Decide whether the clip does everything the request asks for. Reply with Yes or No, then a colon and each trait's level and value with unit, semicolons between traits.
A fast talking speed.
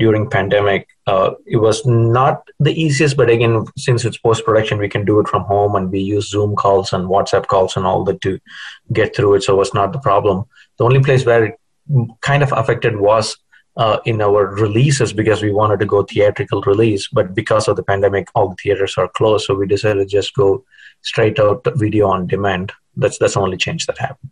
Yes: fast, 215 wpm